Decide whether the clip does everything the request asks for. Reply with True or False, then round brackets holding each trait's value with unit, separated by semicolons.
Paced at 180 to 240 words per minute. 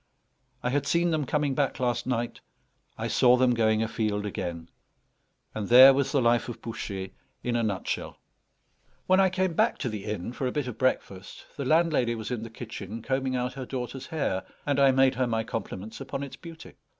True (200 wpm)